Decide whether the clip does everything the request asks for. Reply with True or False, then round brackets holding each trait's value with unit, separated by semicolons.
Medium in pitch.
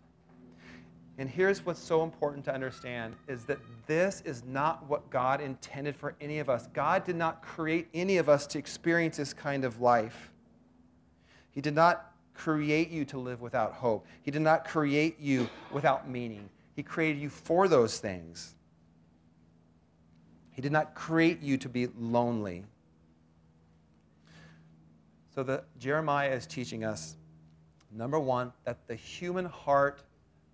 False (130 Hz)